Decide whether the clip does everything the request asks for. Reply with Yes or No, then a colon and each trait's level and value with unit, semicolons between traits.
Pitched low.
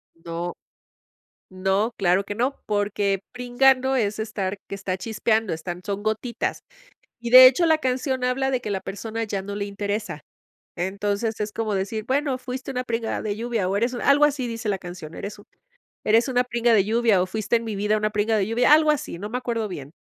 No: high, 220 Hz